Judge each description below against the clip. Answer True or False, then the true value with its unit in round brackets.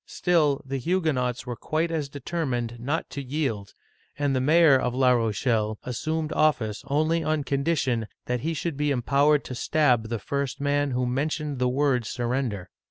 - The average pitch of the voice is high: False (140 Hz)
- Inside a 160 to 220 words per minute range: True (175 wpm)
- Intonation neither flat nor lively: True (3.6 semitones)